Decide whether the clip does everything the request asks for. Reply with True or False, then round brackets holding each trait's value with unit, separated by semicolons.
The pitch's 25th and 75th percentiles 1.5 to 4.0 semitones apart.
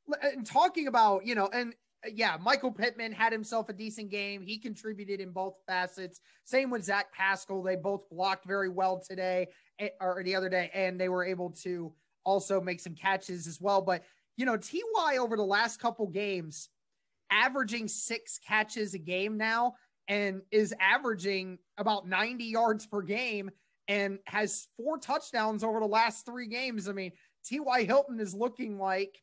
True (3.4 semitones)